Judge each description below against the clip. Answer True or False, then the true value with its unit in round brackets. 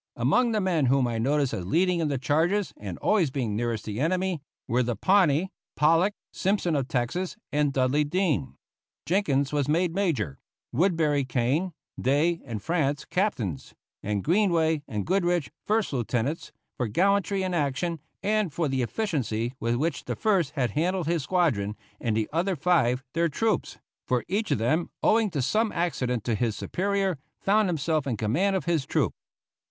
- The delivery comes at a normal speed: True (170 wpm)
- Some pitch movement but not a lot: False (6.4 semitones)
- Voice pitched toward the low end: False (155 Hz)